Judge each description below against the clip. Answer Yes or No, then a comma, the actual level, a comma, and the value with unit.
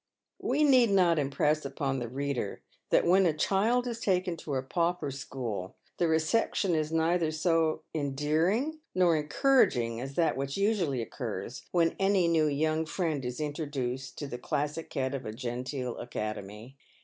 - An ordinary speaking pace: Yes, average, 160 wpm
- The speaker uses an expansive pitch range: No, average, 4.8 semitones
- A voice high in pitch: No, medium, 150 Hz